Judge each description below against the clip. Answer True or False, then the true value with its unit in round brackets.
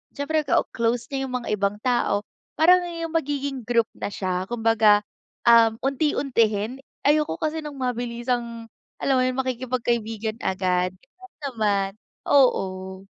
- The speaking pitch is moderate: False (240 Hz)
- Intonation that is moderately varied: True (4.3 semitones)